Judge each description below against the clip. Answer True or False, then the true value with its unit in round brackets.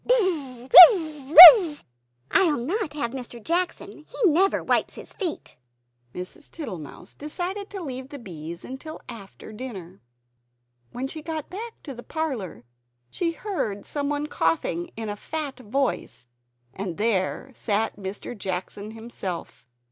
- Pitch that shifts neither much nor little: False (7.9 semitones)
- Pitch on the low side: False (265 Hz)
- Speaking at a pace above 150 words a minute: False (140 wpm)